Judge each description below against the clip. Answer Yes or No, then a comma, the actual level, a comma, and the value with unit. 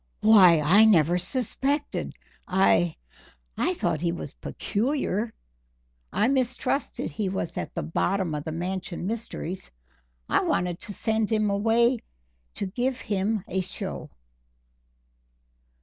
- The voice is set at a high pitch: Yes, high, 200 Hz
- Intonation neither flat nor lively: Yes, average, 4.2 semitones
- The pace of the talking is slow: Yes, slow, 120 wpm